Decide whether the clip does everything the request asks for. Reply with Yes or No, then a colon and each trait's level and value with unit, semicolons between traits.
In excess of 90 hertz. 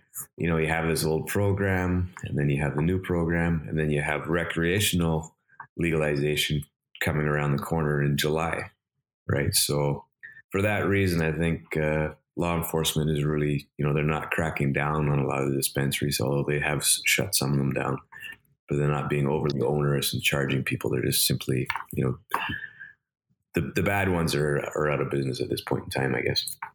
No: very low, 75 Hz